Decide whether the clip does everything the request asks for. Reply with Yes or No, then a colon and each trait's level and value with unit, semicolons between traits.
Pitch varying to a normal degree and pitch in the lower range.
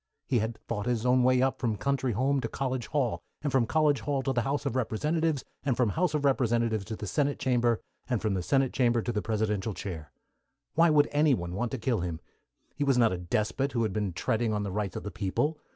Yes: average, 4.3 semitones; low, 120 Hz